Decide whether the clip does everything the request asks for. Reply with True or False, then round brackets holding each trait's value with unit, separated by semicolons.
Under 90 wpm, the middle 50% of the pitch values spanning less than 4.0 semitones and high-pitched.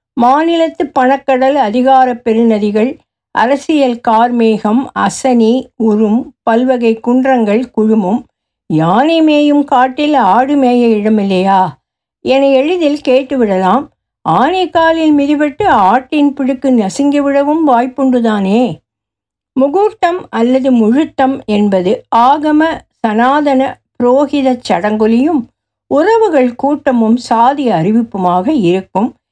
False (80 wpm; 4.3 semitones; 255 Hz)